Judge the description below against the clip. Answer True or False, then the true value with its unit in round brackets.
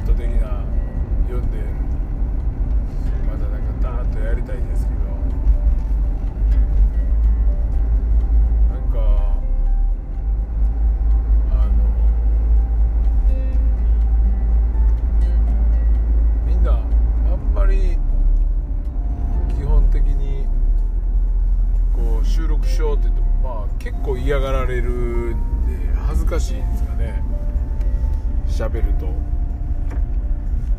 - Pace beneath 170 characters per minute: True (140 characters per minute)